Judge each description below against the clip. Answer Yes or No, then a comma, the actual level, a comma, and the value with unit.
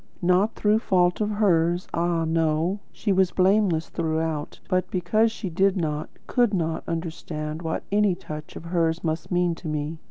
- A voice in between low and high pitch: Yes, medium, 175 Hz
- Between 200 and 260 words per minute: No, average, 165 wpm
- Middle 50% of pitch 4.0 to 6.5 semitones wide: No, average, 3.0 semitones